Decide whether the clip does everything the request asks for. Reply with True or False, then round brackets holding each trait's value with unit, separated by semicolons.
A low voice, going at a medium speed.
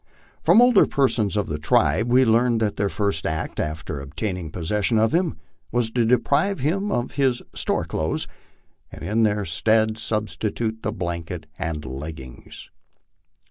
True (110 Hz; 155 wpm)